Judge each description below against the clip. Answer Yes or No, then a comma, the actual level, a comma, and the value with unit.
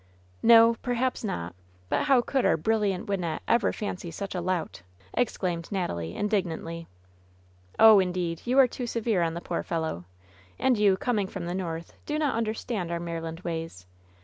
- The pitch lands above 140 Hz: Yes, high, 190 Hz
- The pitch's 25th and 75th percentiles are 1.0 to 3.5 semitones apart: No, average, 5.3 semitones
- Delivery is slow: No, average, 175 wpm